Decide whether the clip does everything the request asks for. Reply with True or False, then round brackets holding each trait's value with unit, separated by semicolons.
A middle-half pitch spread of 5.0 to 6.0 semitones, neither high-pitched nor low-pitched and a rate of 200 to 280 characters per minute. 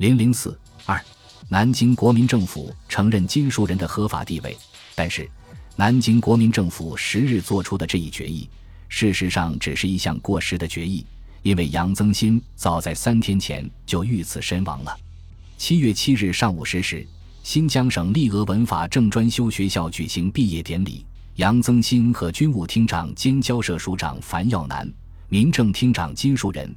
False (5.6 semitones; 100 Hz; 260 characters per minute)